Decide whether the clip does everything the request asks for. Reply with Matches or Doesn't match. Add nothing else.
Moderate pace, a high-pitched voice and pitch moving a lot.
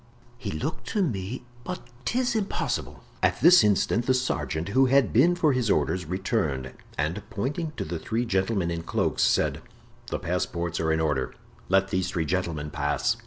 Doesn't match